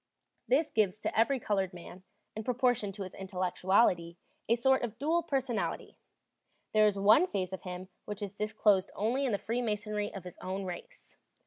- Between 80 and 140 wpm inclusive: No, average, 175 wpm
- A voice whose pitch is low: No, high, 210 Hz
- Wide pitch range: No, average, 4.0 semitones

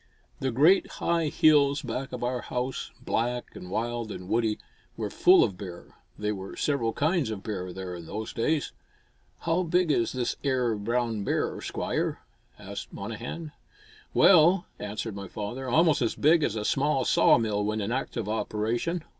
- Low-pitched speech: Yes, low, 120 Hz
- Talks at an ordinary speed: Yes, average, 165 wpm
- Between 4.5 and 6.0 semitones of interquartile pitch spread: Yes, wide, 5.5 semitones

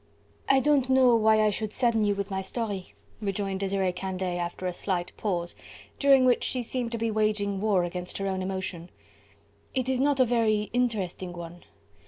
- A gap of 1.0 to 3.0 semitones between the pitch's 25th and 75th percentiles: No, average, 4.0 semitones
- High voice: Yes, high, 205 Hz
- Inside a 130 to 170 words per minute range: No, average, 185 wpm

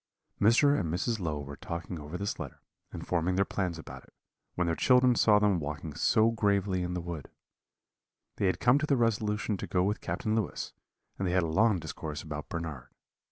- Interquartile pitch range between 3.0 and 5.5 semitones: Yes, average, 4.6 semitones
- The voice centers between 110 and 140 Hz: No, very low, 95 Hz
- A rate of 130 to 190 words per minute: No, fast, 205 wpm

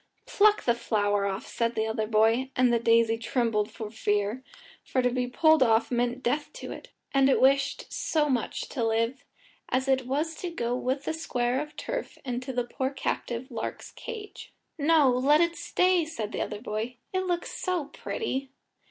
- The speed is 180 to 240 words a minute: Yes, average, 185 wpm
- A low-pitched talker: No, very high, 255 Hz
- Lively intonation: No, average, 4.6 semitones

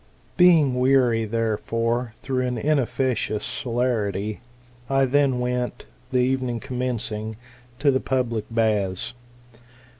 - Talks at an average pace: No, slow, 110 wpm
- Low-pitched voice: Yes, low, 125 Hz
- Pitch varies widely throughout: No, narrow, 2.5 semitones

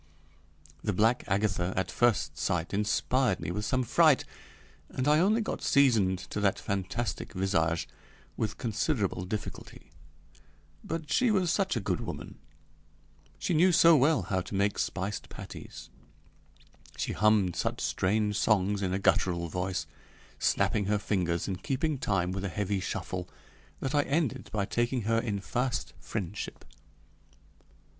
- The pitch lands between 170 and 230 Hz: No, low, 105 Hz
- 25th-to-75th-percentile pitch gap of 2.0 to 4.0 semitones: No, wide, 5.5 semitones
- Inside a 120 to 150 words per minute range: Yes, average, 145 wpm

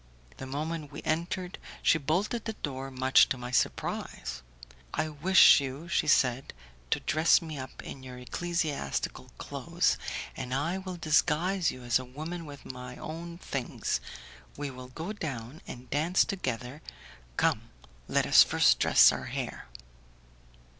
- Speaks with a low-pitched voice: No, medium, 145 Hz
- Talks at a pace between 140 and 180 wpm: Yes, average, 145 wpm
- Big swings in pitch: No, average, 4.5 semitones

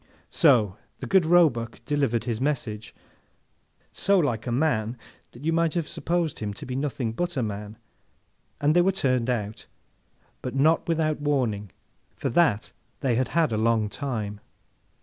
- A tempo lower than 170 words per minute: Yes, average, 155 wpm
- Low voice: Yes, low, 130 Hz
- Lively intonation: Yes, wide, 6.1 semitones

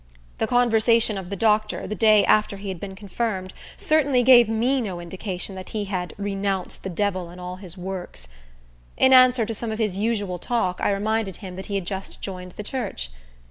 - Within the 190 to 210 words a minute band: Yes, average, 200 wpm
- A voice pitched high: Yes, high, 200 Hz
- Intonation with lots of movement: No, average, 3.2 semitones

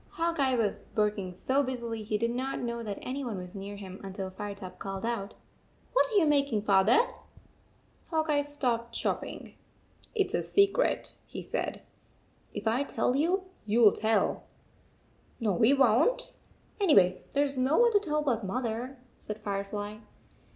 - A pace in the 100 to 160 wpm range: No, average, 180 wpm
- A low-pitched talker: No, high, 235 Hz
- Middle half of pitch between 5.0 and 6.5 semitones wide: Yes, wide, 5.6 semitones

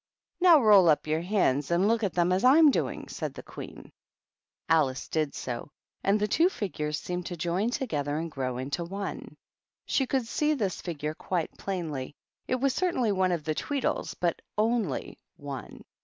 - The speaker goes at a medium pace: Yes, average, 175 wpm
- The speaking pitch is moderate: Yes, medium, 180 Hz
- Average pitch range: No, wide, 6.8 semitones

